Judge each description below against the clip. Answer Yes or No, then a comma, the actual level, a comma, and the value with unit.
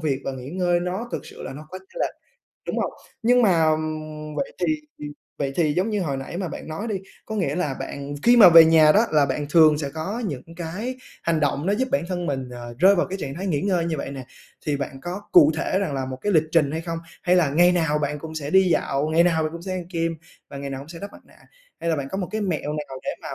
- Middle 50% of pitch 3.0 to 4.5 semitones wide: Yes, average, 4.0 semitones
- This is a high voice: No, medium, 160 Hz